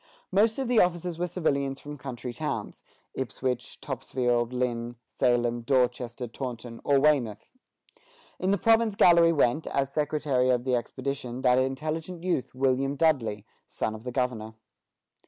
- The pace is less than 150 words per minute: Yes, average, 140 wpm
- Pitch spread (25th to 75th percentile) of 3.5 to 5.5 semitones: Yes, average, 4.1 semitones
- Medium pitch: No, low, 130 Hz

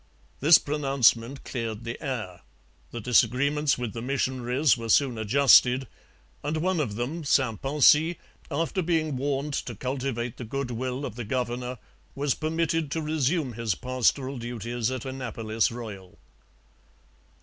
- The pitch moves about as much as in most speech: Yes, average, 3.5 semitones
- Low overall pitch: Yes, low, 130 Hz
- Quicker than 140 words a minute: No, slow, 135 wpm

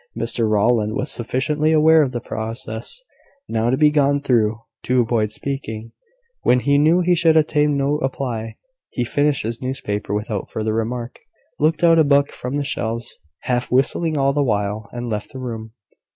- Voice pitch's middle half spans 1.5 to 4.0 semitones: No, average, 4.5 semitones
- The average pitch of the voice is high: No, low, 125 Hz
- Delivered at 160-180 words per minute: Yes, average, 175 wpm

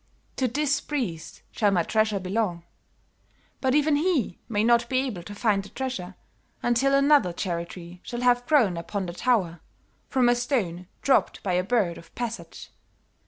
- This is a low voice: No, high, 225 Hz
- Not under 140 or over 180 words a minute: Yes, average, 165 wpm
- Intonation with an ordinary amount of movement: No, wide, 6.1 semitones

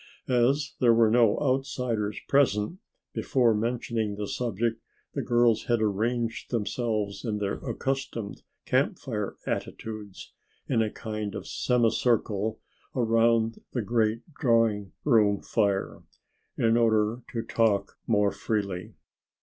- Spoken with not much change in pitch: Yes, narrow, 2.3 semitones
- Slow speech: Yes, slow, 120 wpm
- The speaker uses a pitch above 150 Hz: No, low, 115 Hz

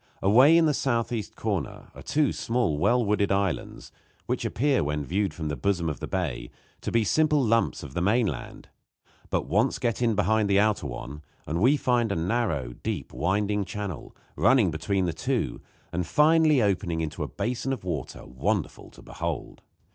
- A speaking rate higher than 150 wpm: Yes, average, 180 wpm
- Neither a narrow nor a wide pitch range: No, wide, 6.6 semitones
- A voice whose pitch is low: Yes, low, 100 Hz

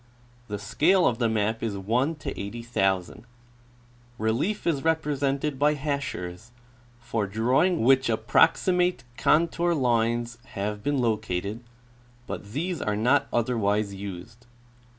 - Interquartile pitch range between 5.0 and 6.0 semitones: Yes, wide, 5.4 semitones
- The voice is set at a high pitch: No, low, 120 Hz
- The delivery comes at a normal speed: No, slow, 110 wpm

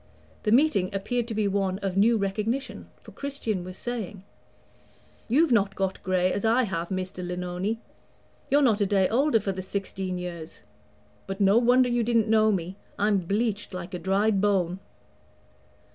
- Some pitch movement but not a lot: Yes, average, 3.4 semitones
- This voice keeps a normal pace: Yes, average, 165 wpm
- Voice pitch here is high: Yes, high, 200 Hz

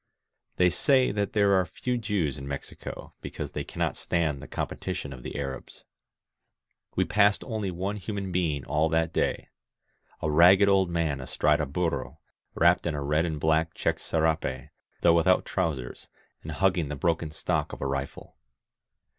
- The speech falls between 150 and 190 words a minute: Yes, average, 170 wpm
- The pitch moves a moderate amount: Yes, average, 4.1 semitones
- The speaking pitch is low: Yes, very low, 80 Hz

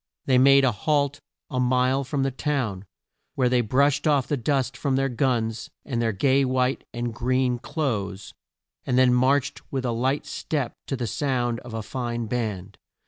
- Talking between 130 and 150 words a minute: No, average, 180 wpm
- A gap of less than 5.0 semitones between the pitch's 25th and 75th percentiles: Yes, narrow, 2.4 semitones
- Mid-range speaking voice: No, low, 130 Hz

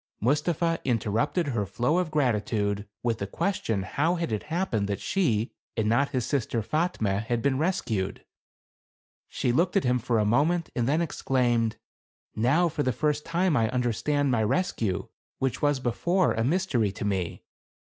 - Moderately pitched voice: No, low, 125 Hz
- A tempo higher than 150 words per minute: Yes, average, 170 wpm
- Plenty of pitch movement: Yes, wide, 6.3 semitones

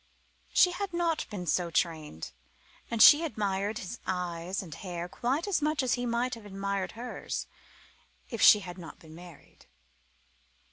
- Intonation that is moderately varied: No, wide, 5.9 semitones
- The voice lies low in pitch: No, high, 200 Hz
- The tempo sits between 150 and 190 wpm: Yes, average, 155 wpm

